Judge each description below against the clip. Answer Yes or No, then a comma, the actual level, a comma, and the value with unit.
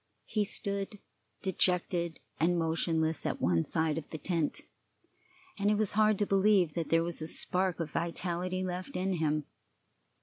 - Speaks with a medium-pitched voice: Yes, medium, 175 Hz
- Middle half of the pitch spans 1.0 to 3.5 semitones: Yes, average, 2.9 semitones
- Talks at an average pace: Yes, average, 160 wpm